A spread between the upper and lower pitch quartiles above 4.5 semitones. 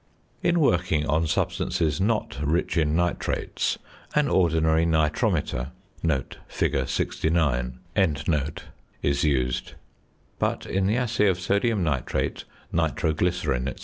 No: average, 4.1 semitones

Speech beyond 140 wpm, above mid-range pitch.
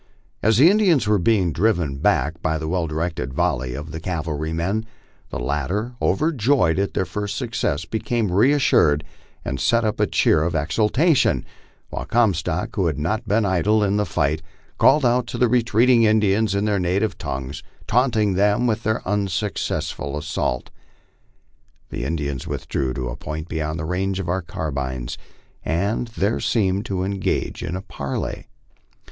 No: average, 160 wpm; very low, 95 Hz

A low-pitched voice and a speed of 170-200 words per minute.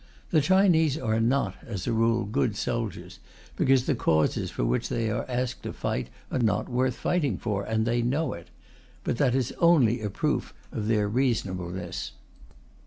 Yes: low, 115 Hz; average, 175 wpm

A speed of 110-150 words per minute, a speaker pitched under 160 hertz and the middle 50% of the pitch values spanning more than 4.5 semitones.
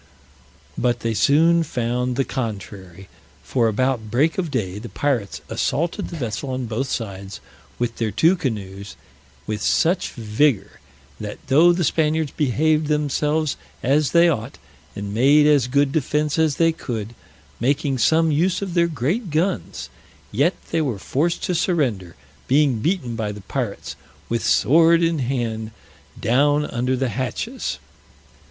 Yes: average, 145 wpm; low, 135 Hz; wide, 5.6 semitones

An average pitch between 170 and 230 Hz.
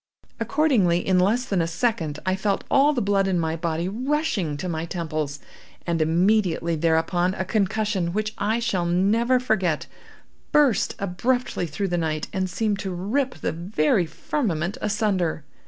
Yes: high, 190 Hz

